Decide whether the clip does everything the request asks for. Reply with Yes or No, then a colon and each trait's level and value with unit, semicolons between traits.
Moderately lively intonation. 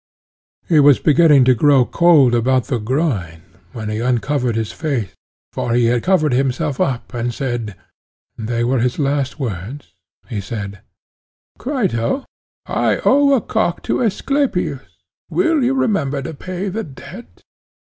No: wide, 6.3 semitones